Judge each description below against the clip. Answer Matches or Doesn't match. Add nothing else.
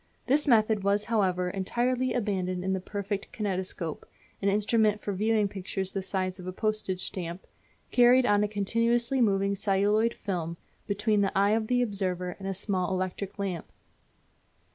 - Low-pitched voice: Doesn't match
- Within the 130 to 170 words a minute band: Matches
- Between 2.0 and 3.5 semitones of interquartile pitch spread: Matches